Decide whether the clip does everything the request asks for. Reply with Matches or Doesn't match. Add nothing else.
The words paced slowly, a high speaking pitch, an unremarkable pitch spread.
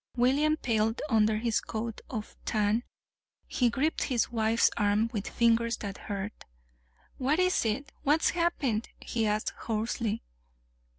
Matches